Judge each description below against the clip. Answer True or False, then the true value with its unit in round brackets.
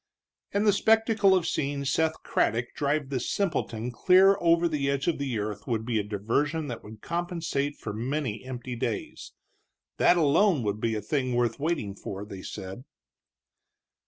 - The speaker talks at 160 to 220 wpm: True (165 wpm)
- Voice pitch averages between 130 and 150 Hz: True (140 Hz)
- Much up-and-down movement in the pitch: True (6.8 semitones)